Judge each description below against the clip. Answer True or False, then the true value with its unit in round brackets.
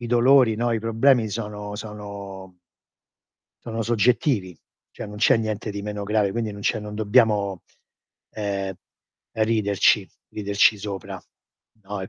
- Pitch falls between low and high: False (105 Hz)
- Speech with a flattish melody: True (2.0 semitones)